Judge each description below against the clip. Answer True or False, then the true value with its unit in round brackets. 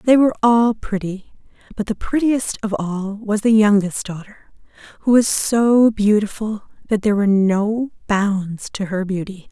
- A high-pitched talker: True (210 Hz)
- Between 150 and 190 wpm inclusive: True (160 wpm)